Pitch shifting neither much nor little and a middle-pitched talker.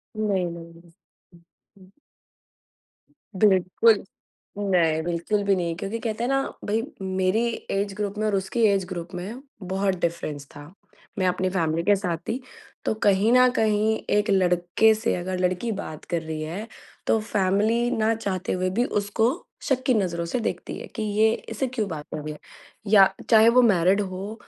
No: average, 3.5 semitones; high, 195 Hz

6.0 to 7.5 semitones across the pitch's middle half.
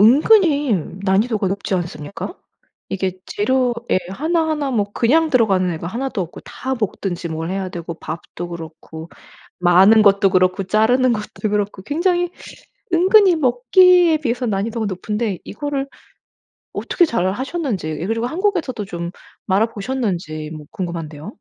Yes: wide, 6.5 semitones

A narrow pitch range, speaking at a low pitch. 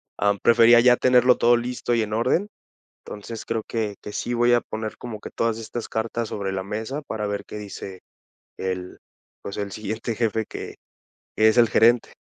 Yes: narrow, 2.3 semitones; low, 110 Hz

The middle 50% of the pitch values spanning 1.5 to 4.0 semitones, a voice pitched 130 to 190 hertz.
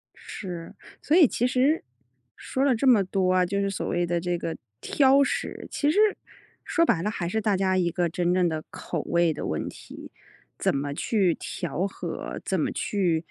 No: average, 5.0 semitones; medium, 185 Hz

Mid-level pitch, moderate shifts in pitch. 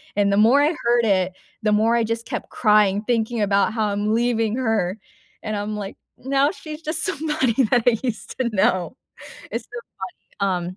No: high, 225 Hz; average, 3.0 semitones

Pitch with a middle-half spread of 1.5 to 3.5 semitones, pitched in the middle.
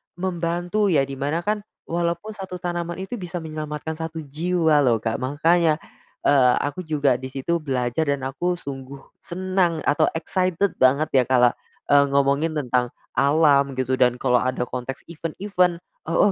No: average, 4.4 semitones; medium, 155 Hz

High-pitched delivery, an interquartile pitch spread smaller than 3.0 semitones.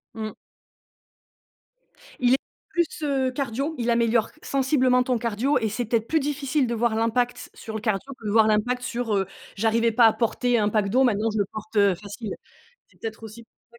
Yes: high, 230 Hz; narrow, 2.5 semitones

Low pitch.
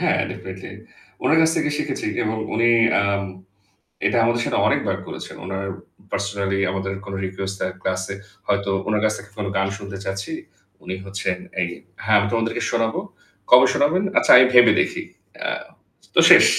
Yes: low, 100 Hz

